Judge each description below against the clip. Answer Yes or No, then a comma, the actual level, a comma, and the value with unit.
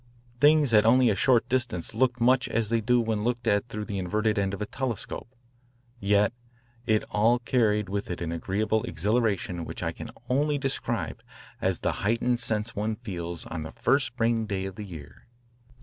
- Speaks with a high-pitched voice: No, low, 110 Hz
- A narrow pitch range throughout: No, average, 3.4 semitones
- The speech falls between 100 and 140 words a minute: No, average, 185 wpm